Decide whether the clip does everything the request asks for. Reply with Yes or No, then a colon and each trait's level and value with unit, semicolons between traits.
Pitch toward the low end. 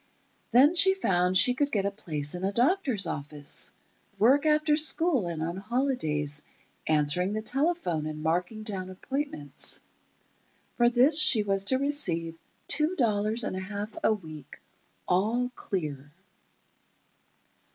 No: high, 205 Hz